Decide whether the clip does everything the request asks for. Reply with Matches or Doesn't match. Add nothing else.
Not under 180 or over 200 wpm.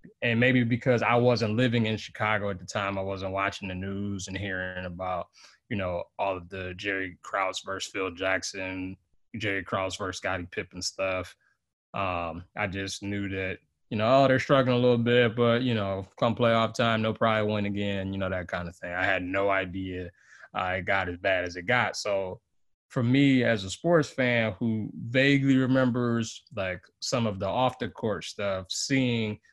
Matches